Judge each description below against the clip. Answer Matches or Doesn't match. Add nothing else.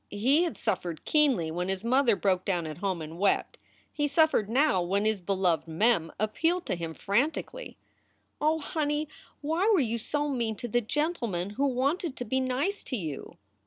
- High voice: Matches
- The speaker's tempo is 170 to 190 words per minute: Matches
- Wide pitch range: Matches